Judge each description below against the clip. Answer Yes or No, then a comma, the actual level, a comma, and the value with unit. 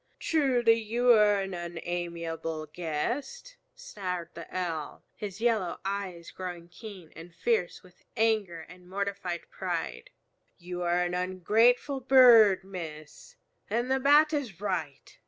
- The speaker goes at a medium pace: No, slow, 125 wpm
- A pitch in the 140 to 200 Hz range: Yes, high, 190 Hz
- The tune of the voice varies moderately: Yes, average, 5.0 semitones